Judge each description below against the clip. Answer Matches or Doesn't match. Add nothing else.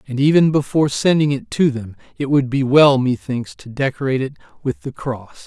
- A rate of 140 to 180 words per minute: Doesn't match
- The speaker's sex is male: Matches